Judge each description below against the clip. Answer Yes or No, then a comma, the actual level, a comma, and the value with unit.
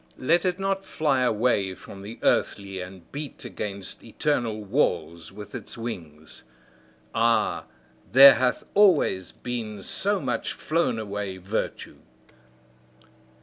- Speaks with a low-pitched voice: Yes, low, 110 Hz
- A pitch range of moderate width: No, wide, 6.0 semitones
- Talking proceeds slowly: Yes, slow, 115 wpm